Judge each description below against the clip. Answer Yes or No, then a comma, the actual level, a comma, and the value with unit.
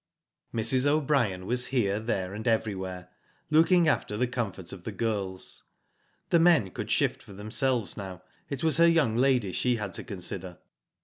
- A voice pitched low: Yes, low, 110 Hz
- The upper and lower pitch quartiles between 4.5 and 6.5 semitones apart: Yes, wide, 5.5 semitones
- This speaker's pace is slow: No, average, 165 wpm